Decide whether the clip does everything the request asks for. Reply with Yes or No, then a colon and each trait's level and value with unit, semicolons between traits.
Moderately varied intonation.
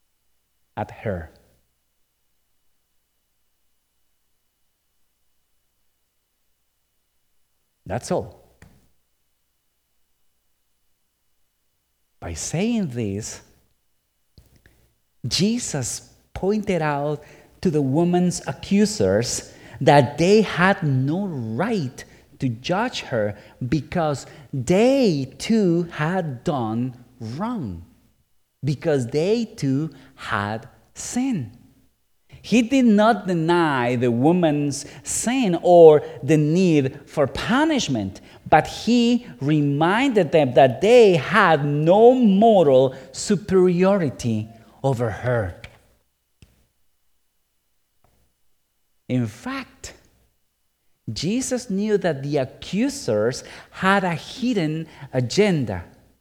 No: wide, 9.0 semitones